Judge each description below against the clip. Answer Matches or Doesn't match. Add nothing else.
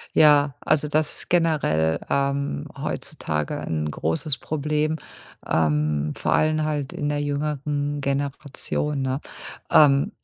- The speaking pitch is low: Doesn't match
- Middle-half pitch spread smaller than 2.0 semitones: Doesn't match